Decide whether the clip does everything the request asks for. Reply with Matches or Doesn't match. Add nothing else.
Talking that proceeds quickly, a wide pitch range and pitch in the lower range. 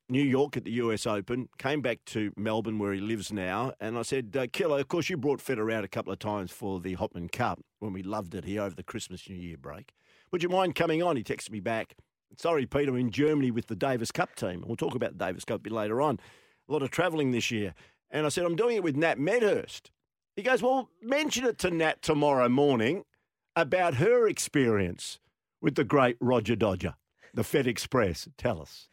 Matches